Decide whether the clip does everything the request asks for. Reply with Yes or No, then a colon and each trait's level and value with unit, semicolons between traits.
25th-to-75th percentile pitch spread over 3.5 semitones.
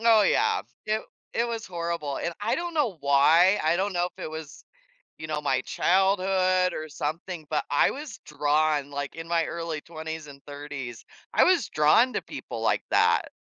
Yes: average, 4.3 semitones